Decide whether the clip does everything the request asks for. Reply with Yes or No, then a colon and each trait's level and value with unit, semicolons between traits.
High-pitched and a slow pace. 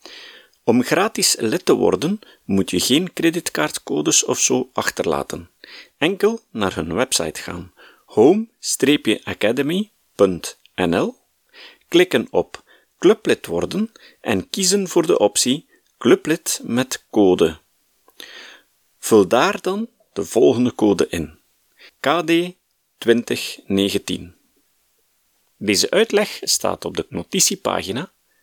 Yes: high, 205 Hz; slow, 95 wpm